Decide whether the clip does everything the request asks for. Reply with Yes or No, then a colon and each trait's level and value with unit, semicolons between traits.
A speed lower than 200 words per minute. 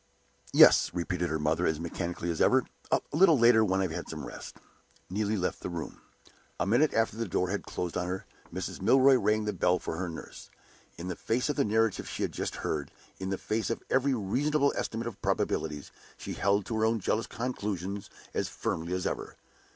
No: fast, 205 wpm